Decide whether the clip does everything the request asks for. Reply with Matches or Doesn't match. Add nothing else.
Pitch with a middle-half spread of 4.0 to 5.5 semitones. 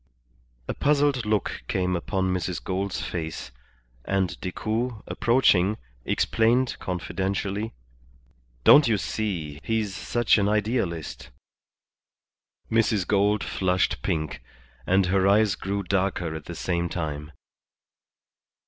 Doesn't match